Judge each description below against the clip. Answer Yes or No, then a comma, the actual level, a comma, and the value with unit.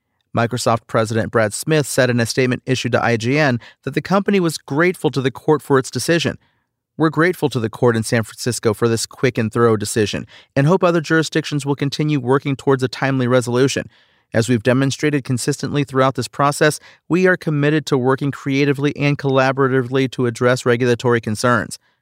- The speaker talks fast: No, average, 180 wpm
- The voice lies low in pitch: Yes, low, 130 Hz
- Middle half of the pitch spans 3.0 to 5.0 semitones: Yes, average, 3.4 semitones